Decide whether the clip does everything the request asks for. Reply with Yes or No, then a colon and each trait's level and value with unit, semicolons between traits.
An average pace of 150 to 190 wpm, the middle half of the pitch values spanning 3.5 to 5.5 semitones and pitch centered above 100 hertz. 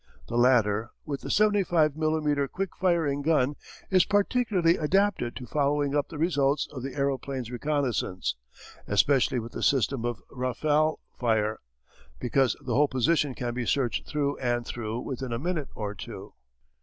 Yes: average, 155 wpm; average, 4.2 semitones; medium, 140 Hz